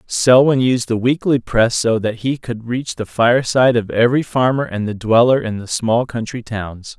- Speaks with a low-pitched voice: Yes, low, 120 Hz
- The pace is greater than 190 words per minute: Yes, average, 200 wpm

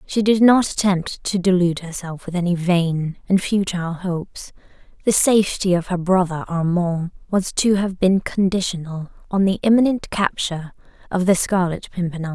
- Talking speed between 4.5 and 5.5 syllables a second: Yes, 5.0 syllables/s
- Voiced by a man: No, female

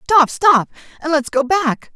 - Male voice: No, female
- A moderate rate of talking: No, slow, 125 wpm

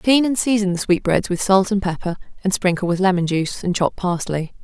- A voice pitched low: No, high, 190 Hz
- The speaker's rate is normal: No, fast, 220 wpm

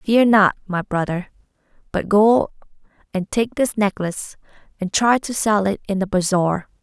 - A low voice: No, high, 200 Hz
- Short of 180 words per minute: Yes, average, 160 wpm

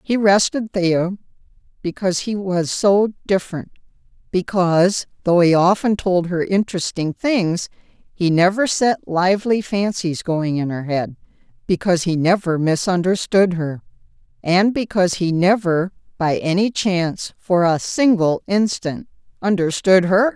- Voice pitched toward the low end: No, medium, 185 Hz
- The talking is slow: Yes, slow, 125 wpm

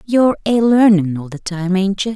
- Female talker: Yes, female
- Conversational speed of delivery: No, fast, 225 wpm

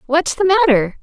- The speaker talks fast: No, average, 175 wpm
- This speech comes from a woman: Yes, female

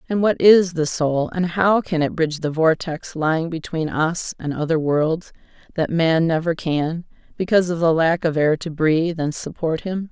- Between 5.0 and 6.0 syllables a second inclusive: No, 4.7 syllables/s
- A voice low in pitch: No, medium, 165 Hz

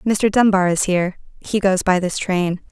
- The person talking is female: Yes, female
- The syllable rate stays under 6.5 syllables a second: Yes, 4.9 syllables/s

